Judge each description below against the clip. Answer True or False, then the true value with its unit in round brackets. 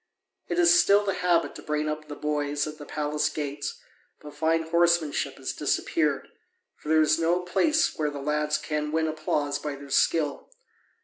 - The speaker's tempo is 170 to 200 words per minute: True (180 wpm)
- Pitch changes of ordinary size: False (2.1 semitones)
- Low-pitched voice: False (155 Hz)